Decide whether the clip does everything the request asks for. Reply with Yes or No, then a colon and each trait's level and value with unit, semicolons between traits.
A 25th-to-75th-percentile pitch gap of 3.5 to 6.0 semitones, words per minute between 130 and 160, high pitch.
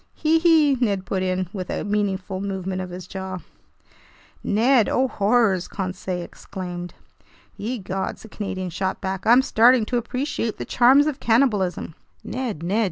Yes: average, 4.6 semitones; average, 155 wpm; high, 200 Hz